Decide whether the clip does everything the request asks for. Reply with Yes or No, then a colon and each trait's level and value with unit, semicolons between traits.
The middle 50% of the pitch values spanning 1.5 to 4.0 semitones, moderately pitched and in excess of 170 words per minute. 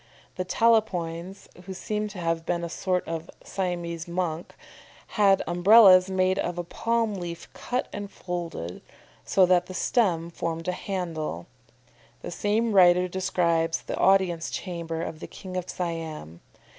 No: narrow, 2.5 semitones; medium, 180 Hz; average, 145 wpm